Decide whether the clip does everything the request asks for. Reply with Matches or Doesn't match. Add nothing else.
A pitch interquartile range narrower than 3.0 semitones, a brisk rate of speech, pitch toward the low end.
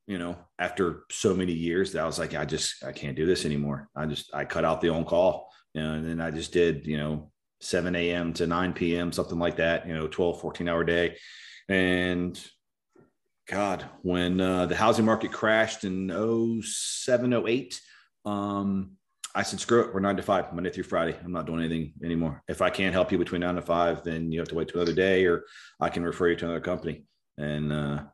Matches